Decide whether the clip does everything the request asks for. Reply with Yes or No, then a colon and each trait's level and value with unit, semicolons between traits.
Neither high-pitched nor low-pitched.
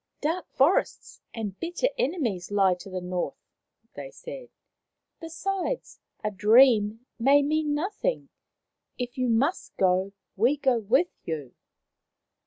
No: very high, 255 Hz